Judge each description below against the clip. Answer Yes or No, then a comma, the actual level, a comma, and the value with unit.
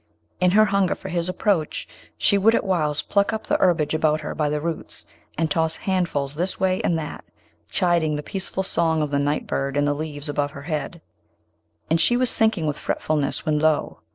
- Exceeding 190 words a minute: Yes, average, 200 wpm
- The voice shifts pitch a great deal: No, average, 3.8 semitones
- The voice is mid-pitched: Yes, medium, 160 Hz